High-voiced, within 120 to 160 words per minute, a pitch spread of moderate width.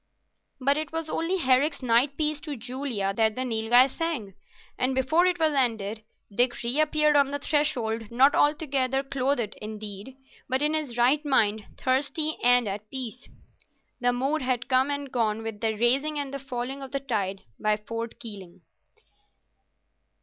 Yes: very high, 255 Hz; average, 155 wpm; average, 4.1 semitones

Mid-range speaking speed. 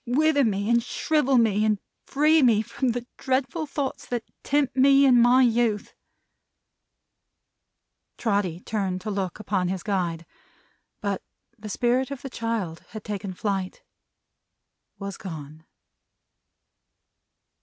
No: slow, 125 wpm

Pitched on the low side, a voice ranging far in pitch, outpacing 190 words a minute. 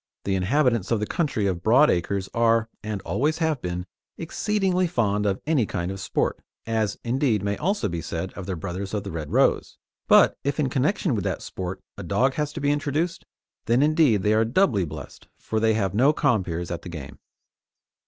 Yes: low, 110 Hz; wide, 7.1 semitones; average, 200 wpm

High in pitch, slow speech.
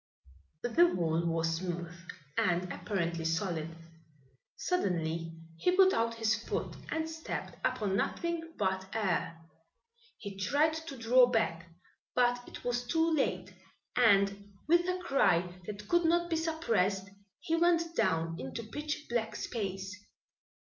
Yes: high, 220 Hz; slow, 130 wpm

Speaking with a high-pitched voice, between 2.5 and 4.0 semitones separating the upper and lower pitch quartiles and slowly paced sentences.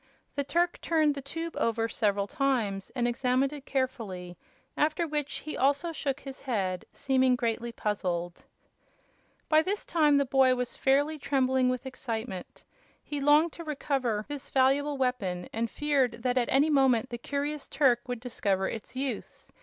No: very high, 265 Hz; average, 3.7 semitones; average, 160 wpm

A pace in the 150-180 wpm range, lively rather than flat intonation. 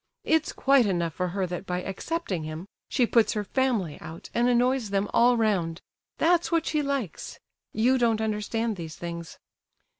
Yes: average, 160 wpm; wide, 6.0 semitones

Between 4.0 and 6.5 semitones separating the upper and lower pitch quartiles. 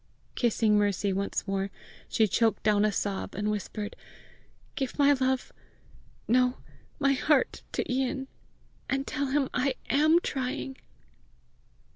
Yes: average, 4.5 semitones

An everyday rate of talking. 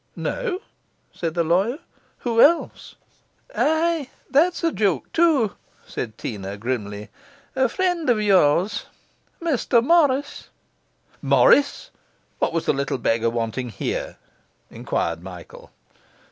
No: slow, 110 wpm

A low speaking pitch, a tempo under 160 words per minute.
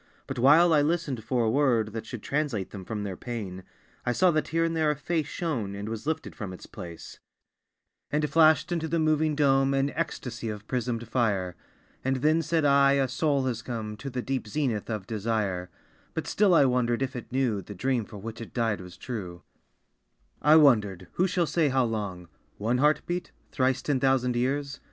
No: low, 130 Hz; average, 200 wpm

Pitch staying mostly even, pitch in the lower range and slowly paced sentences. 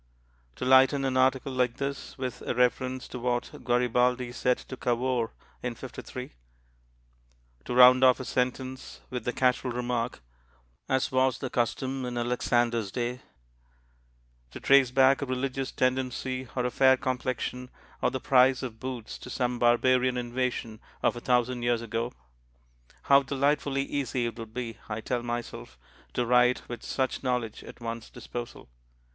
No: narrow, 1.3 semitones; low, 125 Hz; average, 150 wpm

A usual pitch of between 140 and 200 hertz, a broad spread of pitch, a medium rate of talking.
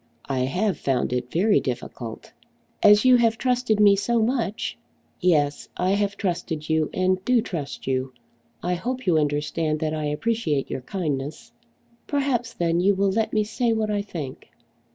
Yes: medium, 185 Hz; wide, 6.5 semitones; average, 170 wpm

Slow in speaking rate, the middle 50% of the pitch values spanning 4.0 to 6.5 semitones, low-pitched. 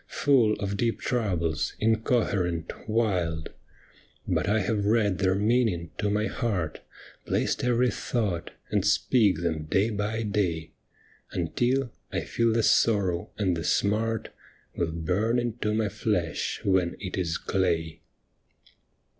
Yes: slow, 130 wpm; average, 4.4 semitones; low, 100 Hz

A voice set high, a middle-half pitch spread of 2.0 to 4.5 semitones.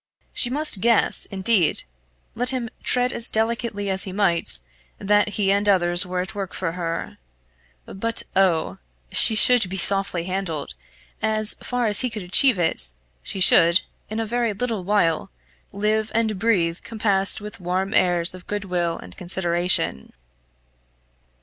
Yes: high, 195 Hz; average, 3.6 semitones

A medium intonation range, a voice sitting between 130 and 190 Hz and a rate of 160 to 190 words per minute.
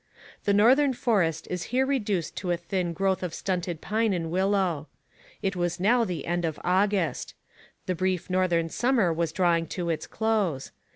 Yes: average, 3.4 semitones; medium, 185 Hz; average, 170 wpm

